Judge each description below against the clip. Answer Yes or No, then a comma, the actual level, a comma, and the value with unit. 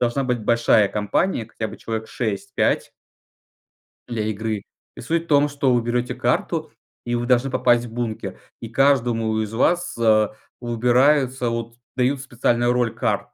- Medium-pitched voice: No, low, 120 Hz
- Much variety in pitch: No, narrow, 2.4 semitones